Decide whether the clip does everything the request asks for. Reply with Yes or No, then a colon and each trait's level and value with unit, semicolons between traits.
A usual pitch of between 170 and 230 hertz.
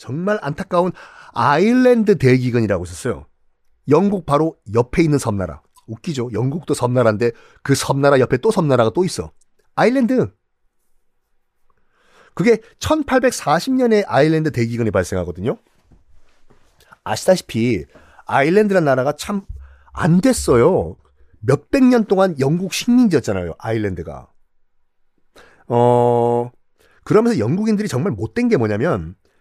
No: low, 135 Hz